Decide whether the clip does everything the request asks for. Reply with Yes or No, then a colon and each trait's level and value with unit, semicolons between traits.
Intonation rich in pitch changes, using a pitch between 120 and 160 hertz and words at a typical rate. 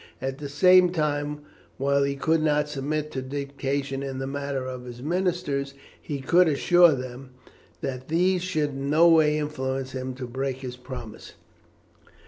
No: narrow, 2.6 semitones; medium, 140 Hz; average, 160 wpm